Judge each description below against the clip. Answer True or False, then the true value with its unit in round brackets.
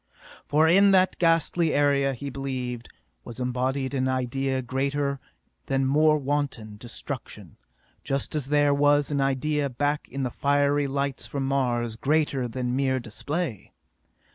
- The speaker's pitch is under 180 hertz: True (140 Hz)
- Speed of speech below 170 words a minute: True (140 wpm)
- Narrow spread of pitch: True (2.0 semitones)